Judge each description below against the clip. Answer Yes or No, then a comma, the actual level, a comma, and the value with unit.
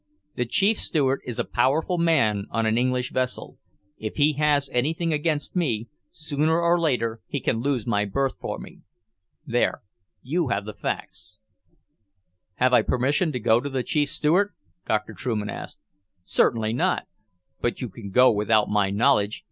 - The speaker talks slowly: No, average, 165 wpm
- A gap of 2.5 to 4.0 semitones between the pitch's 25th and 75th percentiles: No, average, 5.3 semitones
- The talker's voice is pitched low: Yes, low, 125 Hz